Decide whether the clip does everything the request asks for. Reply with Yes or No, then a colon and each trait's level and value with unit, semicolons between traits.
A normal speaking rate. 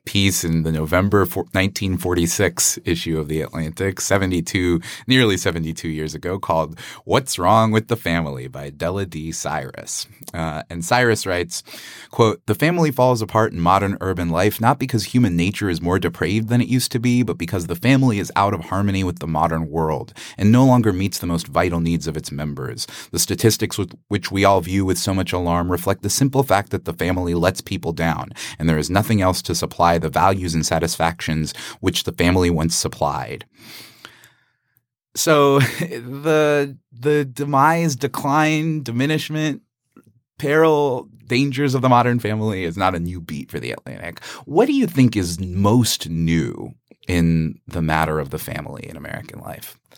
Yes: average, 175 wpm